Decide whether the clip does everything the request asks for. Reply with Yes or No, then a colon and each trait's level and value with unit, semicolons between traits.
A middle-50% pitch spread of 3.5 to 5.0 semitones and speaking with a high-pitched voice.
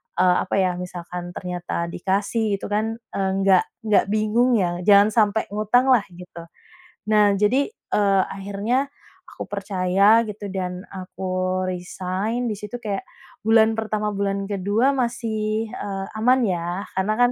No: average, 2.8 semitones; high, 200 Hz